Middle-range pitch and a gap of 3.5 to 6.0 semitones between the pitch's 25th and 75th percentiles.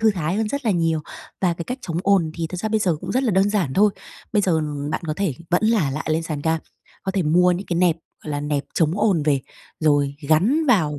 Yes: medium, 170 Hz; average, 4.6 semitones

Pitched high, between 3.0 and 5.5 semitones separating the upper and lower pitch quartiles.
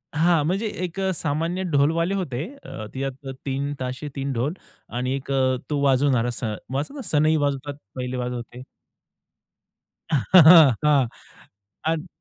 No: medium, 140 Hz; average, 3.5 semitones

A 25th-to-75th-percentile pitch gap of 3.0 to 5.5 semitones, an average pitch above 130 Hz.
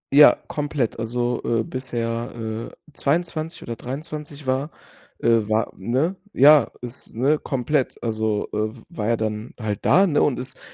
No: average, 4.4 semitones; low, 125 Hz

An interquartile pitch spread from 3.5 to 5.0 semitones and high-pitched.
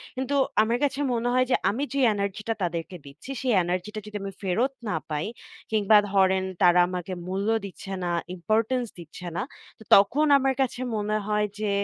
Yes: average, 4.6 semitones; high, 210 Hz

